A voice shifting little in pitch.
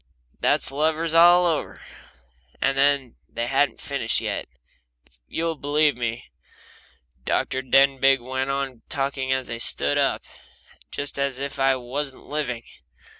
Yes: narrow, 2.0 semitones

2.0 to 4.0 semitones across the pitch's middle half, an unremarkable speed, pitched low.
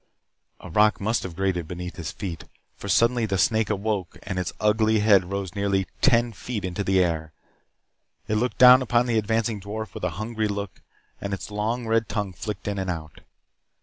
Yes: average, 2.9 semitones; average, 190 wpm; low, 105 Hz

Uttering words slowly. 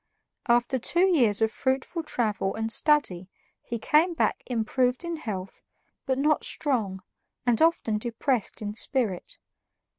Yes: slow, 130 wpm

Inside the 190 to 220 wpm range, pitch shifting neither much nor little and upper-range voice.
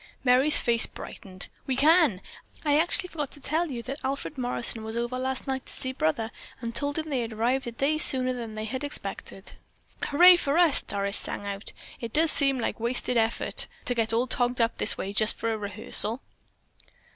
Yes: average, 200 wpm; average, 4.0 semitones; very high, 250 Hz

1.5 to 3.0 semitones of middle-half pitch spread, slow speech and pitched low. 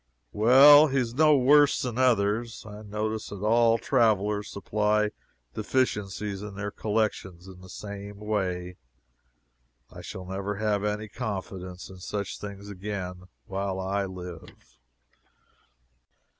Yes: narrow, 2.4 semitones; slow, 125 wpm; low, 105 Hz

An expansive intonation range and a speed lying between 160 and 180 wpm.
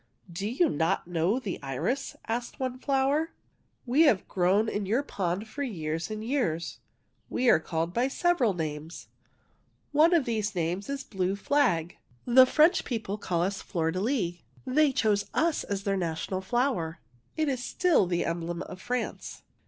Yes: wide, 7.1 semitones; average, 175 wpm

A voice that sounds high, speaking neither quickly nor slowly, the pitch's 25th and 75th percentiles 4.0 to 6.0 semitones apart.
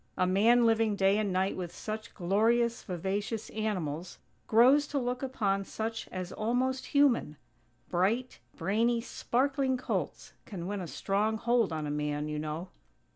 Yes: high, 215 Hz; average, 150 wpm; average, 4.5 semitones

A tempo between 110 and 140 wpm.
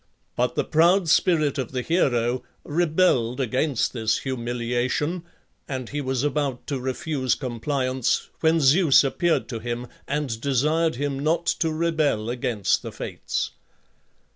Yes: slow, 135 wpm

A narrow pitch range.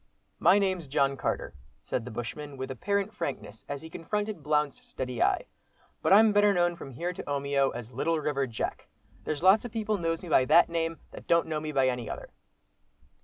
No: average, 4.7 semitones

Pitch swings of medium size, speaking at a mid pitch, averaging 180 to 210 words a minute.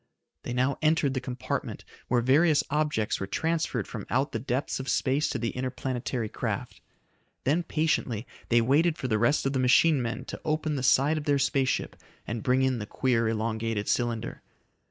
No: average, 3.8 semitones; low, 130 Hz; average, 185 wpm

